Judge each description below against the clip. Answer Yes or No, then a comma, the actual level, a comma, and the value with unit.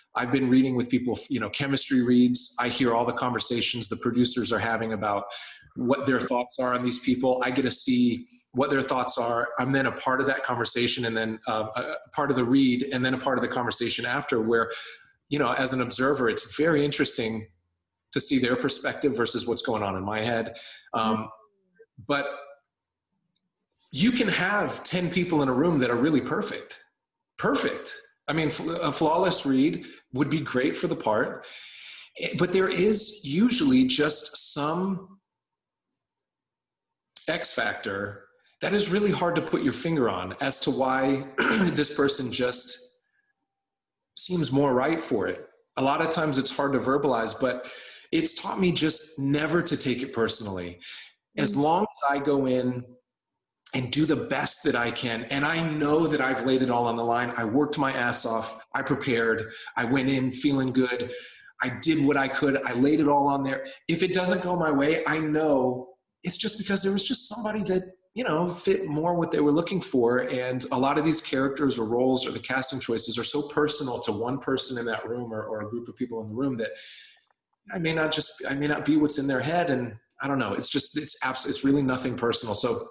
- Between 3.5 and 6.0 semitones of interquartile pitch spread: Yes, average, 4.7 semitones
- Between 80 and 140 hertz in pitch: Yes, low, 135 Hz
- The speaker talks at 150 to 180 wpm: No, average, 200 wpm